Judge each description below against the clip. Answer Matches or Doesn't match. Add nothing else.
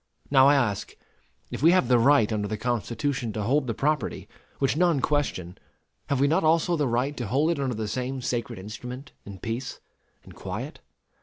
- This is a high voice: Doesn't match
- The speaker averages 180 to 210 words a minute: Matches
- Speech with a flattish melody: Doesn't match